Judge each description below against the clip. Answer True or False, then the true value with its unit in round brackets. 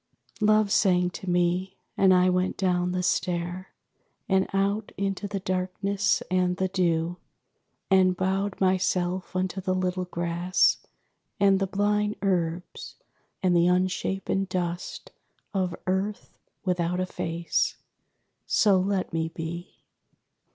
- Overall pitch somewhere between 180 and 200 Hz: True (185 Hz)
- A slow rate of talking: True (125 wpm)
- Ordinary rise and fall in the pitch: False (1.5 semitones)